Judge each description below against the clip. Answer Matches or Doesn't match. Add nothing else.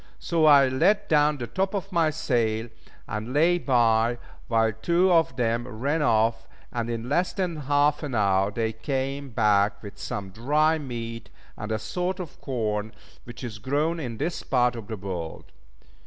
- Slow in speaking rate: Doesn't match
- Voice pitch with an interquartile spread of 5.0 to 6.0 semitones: Matches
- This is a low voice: Matches